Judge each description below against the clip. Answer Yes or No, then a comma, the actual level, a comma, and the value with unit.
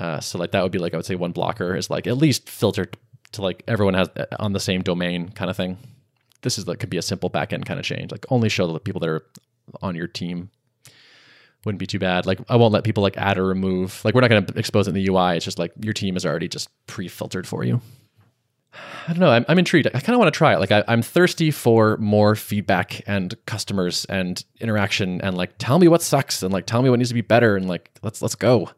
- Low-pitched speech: Yes, low, 105 Hz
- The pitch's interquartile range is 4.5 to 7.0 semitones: Yes, average, 4.9 semitones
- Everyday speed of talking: No, fast, 265 wpm